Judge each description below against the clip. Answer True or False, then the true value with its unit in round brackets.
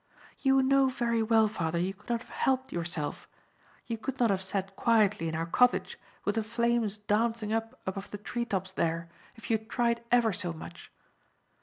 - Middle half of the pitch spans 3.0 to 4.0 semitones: True (3.7 semitones)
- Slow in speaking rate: False (190 wpm)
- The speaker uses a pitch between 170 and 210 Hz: False (220 Hz)